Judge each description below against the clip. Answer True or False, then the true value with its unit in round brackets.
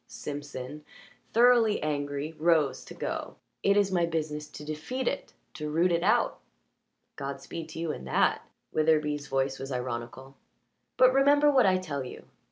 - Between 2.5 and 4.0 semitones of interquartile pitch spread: False (4.8 semitones)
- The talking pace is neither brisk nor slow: True (155 wpm)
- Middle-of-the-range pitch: True (155 Hz)